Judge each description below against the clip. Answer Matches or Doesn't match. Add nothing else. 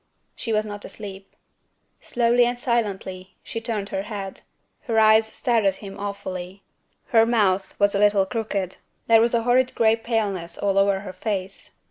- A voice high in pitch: Matches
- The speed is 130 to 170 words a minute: Matches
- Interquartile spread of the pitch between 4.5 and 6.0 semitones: Doesn't match